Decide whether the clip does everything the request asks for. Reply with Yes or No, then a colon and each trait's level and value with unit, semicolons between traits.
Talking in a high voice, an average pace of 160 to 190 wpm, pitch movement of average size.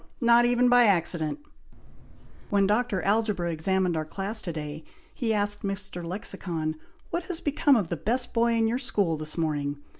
No: high, 200 Hz; average, 170 wpm; wide, 5.9 semitones